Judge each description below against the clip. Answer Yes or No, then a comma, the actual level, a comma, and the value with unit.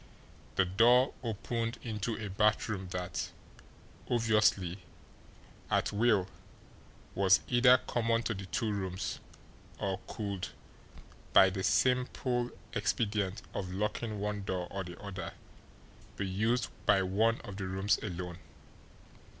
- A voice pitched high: No, low, 105 Hz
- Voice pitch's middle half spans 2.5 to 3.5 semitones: Yes, average, 3.2 semitones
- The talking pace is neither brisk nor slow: No, slow, 120 wpm